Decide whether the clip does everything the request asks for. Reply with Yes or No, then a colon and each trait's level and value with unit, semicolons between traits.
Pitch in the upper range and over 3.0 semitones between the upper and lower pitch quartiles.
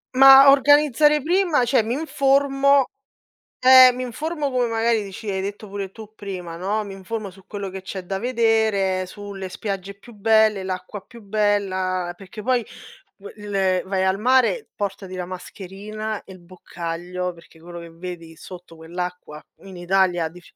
Yes: high, 200 Hz; average, 4.2 semitones